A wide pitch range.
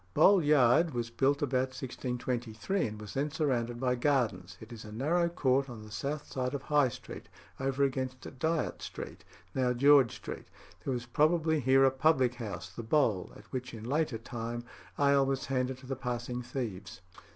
No: average, 2.8 semitones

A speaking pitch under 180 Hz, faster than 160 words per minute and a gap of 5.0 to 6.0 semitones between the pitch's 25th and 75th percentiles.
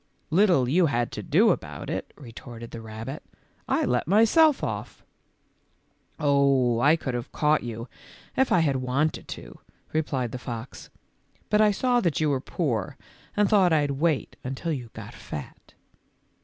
Yes: medium, 140 Hz; average, 170 wpm; wide, 5.5 semitones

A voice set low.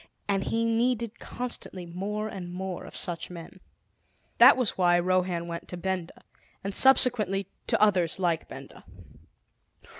No: high, 190 Hz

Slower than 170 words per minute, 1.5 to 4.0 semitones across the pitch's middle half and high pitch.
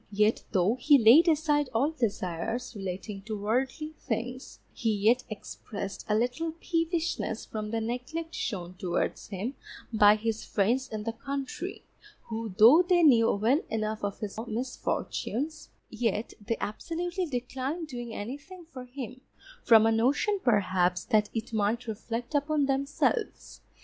No: average, 140 wpm; average, 4.9 semitones; high, 235 Hz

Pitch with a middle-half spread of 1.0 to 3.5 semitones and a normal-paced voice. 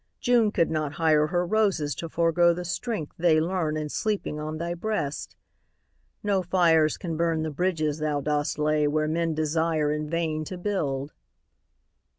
Yes: narrow, 2.5 semitones; average, 165 wpm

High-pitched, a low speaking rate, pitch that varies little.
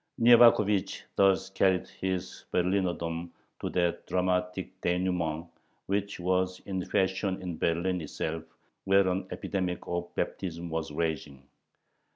No: very low, 90 Hz; slow, 115 wpm; narrow, 1.9 semitones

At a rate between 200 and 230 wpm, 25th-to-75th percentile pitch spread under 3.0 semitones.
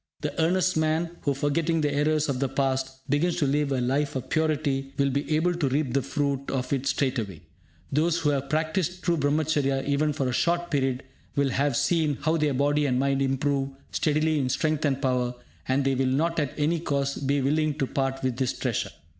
Yes: fast, 205 wpm; narrow, 2.5 semitones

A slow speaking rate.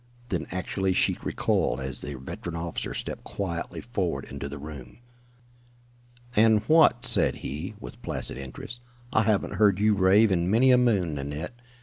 No: average, 155 wpm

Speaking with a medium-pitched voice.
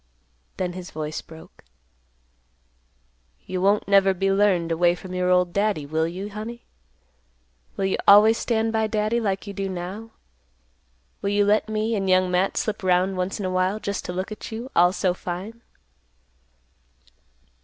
No: high, 195 Hz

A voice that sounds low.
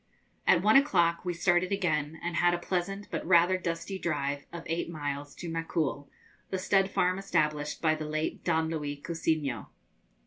No: medium, 170 Hz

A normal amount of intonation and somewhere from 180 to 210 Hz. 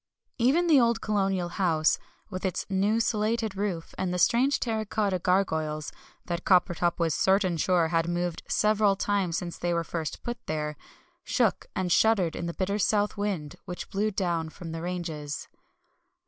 Yes: average, 3.7 semitones; medium, 185 Hz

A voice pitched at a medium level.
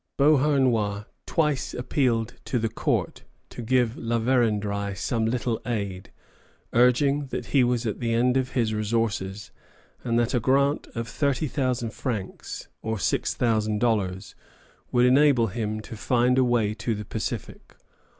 No: low, 120 Hz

